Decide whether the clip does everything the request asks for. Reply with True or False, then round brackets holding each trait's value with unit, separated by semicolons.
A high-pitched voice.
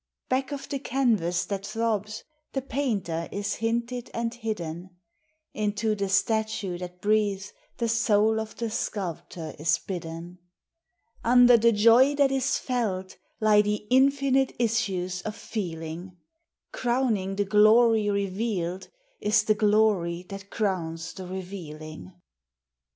True (210 Hz)